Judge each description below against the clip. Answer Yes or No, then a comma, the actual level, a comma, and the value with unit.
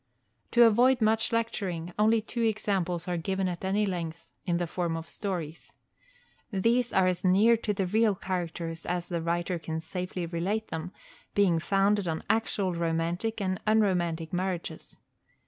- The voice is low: No, medium, 185 Hz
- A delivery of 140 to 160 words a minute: Yes, average, 155 wpm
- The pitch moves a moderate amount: Yes, average, 3.6 semitones